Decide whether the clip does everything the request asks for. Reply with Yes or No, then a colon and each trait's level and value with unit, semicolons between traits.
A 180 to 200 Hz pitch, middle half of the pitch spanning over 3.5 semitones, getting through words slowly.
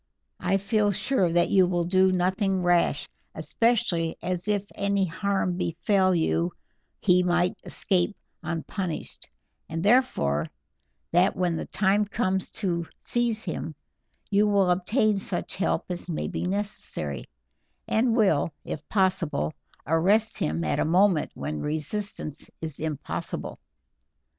No: medium, 185 Hz; average, 3.2 semitones; slow, 130 wpm